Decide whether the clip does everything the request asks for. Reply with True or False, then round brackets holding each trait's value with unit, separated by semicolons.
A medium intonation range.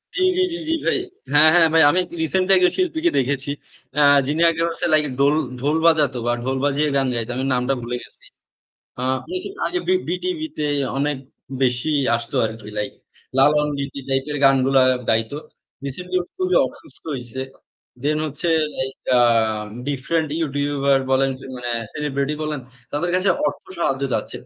True (3.7 semitones)